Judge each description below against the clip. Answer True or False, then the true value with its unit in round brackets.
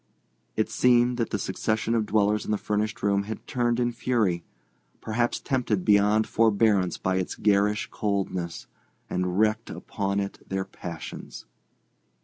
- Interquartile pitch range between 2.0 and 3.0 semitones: True (2.4 semitones)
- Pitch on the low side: True (105 Hz)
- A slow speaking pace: True (130 wpm)